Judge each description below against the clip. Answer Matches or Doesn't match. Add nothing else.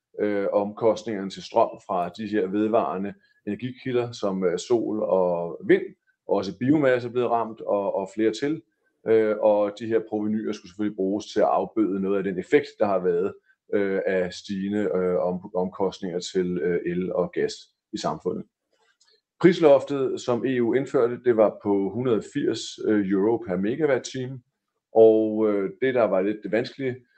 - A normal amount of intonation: Matches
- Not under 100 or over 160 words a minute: Matches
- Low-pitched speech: Matches